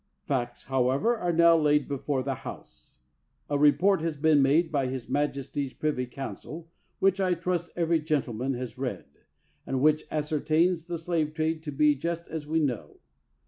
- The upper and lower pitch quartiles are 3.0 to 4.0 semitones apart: Yes, average, 3.5 semitones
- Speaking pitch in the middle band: Yes, medium, 150 Hz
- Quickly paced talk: No, average, 170 wpm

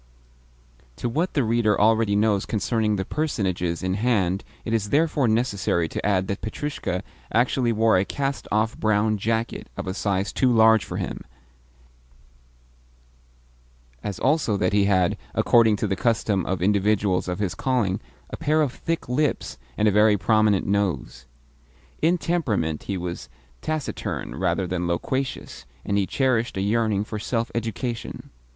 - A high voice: No, low, 105 Hz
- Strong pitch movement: No, average, 3.5 semitones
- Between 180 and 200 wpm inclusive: No, average, 155 wpm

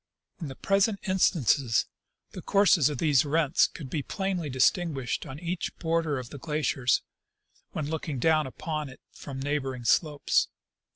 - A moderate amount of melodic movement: Yes, average, 3.7 semitones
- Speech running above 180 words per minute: No, average, 150 wpm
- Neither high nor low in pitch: Yes, medium, 150 Hz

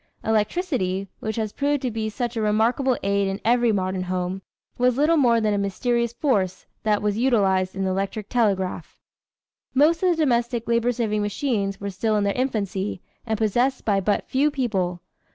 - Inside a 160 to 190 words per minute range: Yes, average, 180 wpm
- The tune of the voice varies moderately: Yes, average, 3.8 semitones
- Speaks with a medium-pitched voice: No, high, 220 Hz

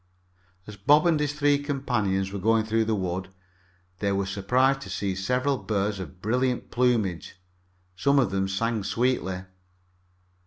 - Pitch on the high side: No, low, 110 Hz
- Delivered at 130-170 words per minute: Yes, average, 150 wpm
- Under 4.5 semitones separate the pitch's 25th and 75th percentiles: No, average, 4.9 semitones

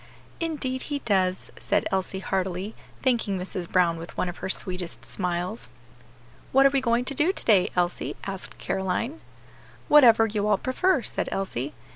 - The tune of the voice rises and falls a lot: Yes, wide, 5.9 semitones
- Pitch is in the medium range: No, high, 195 Hz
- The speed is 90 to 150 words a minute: No, average, 160 wpm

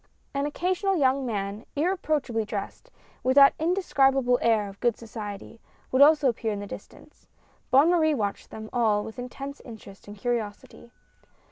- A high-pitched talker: Yes, high, 245 Hz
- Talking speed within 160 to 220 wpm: No, average, 150 wpm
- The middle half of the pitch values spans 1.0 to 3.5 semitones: No, average, 4.8 semitones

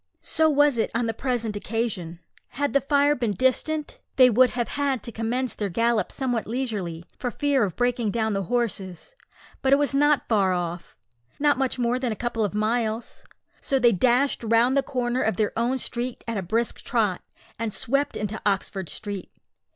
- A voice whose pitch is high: Yes, high, 235 Hz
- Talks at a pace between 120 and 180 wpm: No, average, 190 wpm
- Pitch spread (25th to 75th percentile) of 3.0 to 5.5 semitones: Yes, average, 3.5 semitones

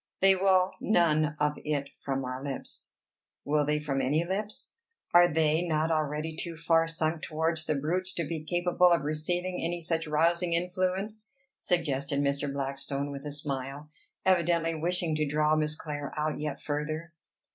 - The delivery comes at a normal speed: Yes, average, 160 wpm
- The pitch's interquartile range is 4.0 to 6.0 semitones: No, average, 2.8 semitones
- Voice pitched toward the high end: No, medium, 155 Hz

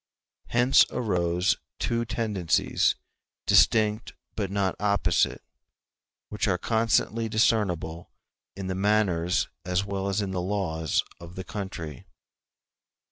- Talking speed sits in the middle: No, slow, 110 wpm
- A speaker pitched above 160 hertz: No, low, 100 Hz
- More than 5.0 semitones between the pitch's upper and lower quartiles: No, average, 3.3 semitones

